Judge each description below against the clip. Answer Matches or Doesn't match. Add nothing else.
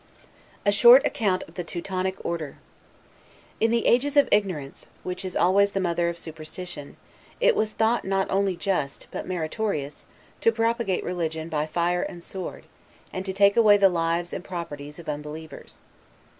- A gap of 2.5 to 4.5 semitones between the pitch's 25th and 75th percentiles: Matches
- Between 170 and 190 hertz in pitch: Matches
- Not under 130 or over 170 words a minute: Matches